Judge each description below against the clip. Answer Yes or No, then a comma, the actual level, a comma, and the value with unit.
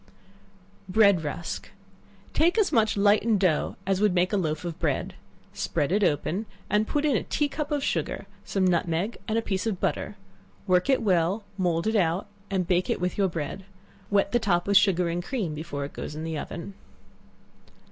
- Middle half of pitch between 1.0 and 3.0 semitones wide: No, average, 3.9 semitones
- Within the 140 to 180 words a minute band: No, average, 190 wpm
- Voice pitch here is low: No, high, 190 Hz